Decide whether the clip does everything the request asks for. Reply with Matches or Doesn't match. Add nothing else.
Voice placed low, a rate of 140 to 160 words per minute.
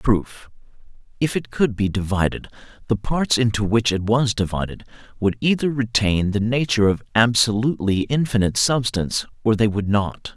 Matches